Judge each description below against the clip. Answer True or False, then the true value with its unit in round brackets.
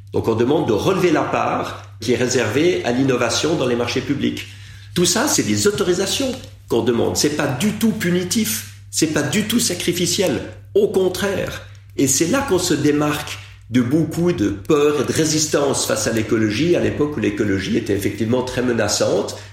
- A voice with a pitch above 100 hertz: True (135 Hz)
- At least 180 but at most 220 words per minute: True (185 wpm)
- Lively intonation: True (8.5 semitones)